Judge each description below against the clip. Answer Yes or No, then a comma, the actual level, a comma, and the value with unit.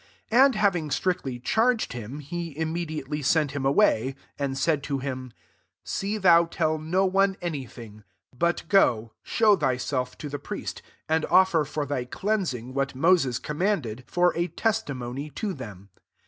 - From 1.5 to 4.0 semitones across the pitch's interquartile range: No, wide, 5.5 semitones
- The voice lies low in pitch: No, medium, 150 Hz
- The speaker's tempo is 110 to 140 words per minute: No, average, 165 wpm